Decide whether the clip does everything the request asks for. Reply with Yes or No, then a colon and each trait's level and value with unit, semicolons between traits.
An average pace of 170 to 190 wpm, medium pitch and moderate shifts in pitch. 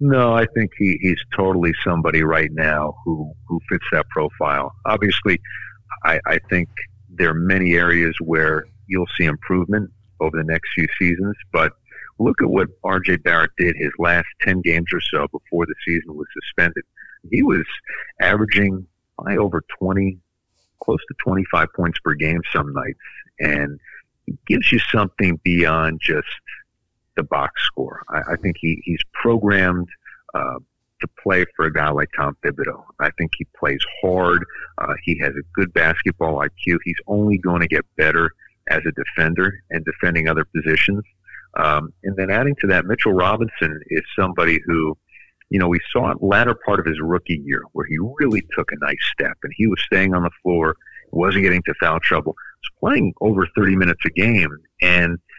No: average, 180 wpm; very low, 90 Hz; average, 3.0 semitones